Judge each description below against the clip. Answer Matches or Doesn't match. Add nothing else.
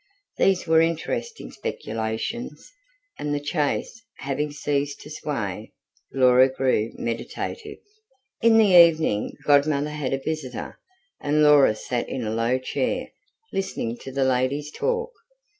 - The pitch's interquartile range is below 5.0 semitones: Matches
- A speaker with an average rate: Doesn't match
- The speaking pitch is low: Doesn't match